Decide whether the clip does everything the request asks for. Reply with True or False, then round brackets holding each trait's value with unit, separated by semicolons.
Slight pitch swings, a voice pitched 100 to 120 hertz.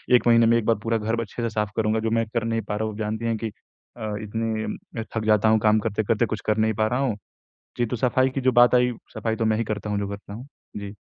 True (1.4 semitones; 110 Hz)